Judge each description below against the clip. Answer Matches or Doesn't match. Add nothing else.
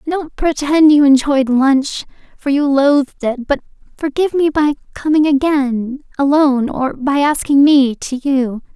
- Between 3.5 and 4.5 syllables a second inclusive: Matches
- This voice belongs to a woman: Matches